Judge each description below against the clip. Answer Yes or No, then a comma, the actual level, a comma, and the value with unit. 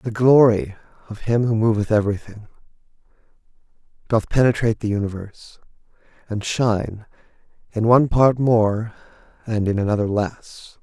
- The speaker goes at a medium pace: No, slow, 115 wpm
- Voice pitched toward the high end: No, low, 110 Hz